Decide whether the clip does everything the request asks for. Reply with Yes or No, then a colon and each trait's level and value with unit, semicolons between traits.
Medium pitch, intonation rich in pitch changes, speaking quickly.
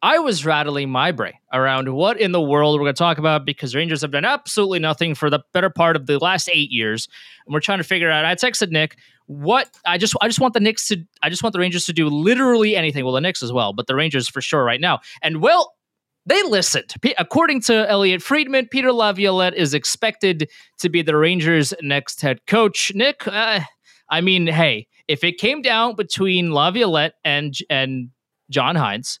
Yes: medium, 170 Hz; wide, 6.1 semitones; fast, 215 wpm